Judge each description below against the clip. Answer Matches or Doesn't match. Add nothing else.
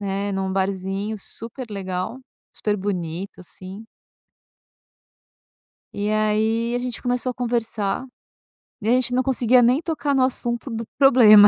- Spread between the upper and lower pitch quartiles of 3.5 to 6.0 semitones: Matches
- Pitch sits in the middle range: Doesn't match